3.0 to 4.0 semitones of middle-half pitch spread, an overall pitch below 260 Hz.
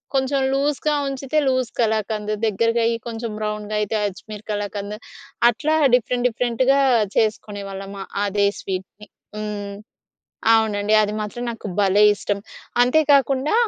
Yes: average, 3.4 semitones; high, 215 Hz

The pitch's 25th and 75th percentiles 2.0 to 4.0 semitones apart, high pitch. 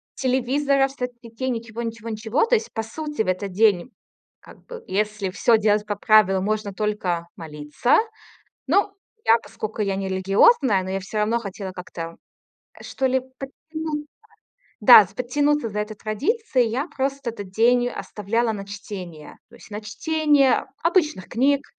No: average, 4.9 semitones; high, 225 Hz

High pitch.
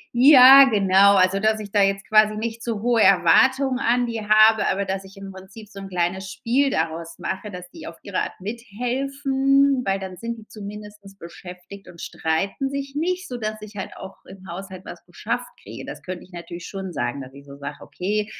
Yes: high, 205 Hz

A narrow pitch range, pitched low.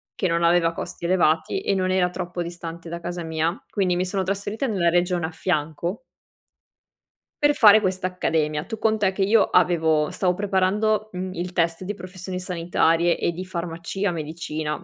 No: narrow, 2.3 semitones; medium, 180 Hz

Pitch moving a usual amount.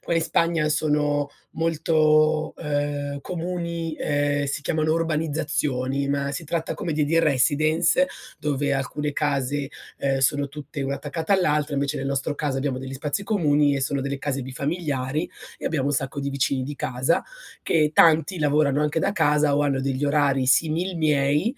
No: narrow, 2.1 semitones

